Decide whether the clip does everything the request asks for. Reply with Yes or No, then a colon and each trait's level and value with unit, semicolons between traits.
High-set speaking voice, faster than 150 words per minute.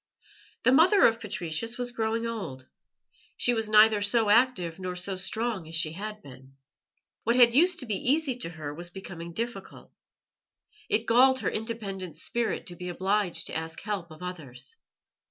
Yes: high, 210 Hz; average, 170 wpm